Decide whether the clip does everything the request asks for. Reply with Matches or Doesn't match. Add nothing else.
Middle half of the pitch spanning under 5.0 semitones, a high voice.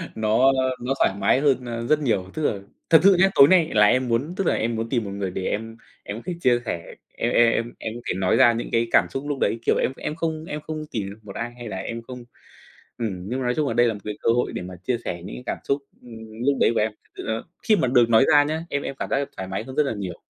Doesn't match